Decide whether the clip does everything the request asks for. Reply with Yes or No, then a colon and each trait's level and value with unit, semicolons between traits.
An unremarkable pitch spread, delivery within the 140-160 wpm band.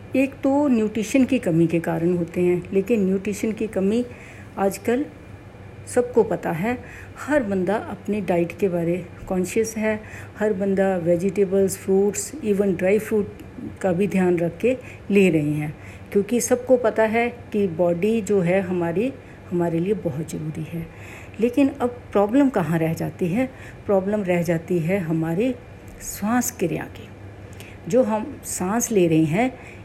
Yes: average, 4.4 semitones; average, 150 wpm